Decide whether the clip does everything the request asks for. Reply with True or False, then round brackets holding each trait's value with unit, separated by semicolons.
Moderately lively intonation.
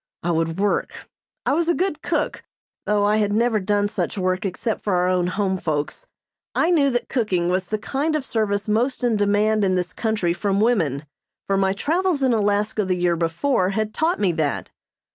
True (4.5 semitones)